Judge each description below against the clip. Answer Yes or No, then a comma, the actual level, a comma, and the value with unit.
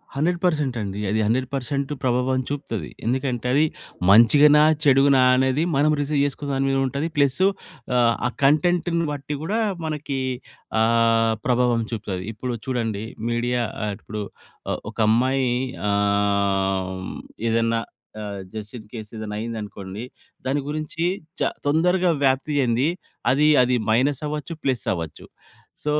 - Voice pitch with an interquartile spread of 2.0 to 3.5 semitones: No, average, 4.7 semitones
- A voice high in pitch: No, low, 130 Hz